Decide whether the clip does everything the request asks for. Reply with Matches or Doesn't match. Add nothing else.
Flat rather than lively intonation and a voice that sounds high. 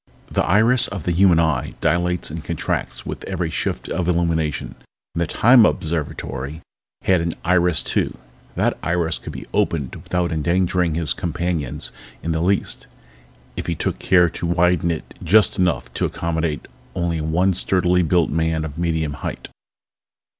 Doesn't match